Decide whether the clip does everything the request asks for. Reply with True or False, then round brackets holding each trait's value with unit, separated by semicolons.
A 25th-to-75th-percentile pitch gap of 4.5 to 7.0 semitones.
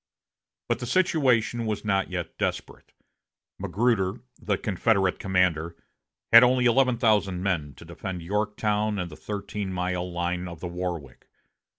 False (3.6 semitones)